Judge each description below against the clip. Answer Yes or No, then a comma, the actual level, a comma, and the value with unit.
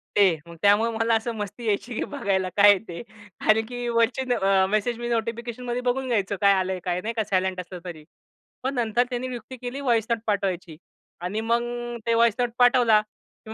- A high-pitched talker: Yes, high, 225 Hz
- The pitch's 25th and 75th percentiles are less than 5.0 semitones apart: Yes, average, 3.4 semitones